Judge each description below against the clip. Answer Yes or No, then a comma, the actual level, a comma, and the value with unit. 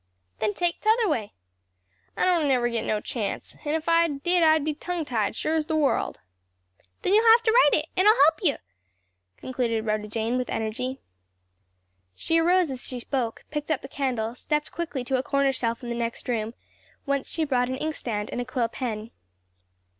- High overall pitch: Yes, very high, 270 Hz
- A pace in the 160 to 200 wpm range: Yes, average, 195 wpm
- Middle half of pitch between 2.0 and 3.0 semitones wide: No, average, 5.2 semitones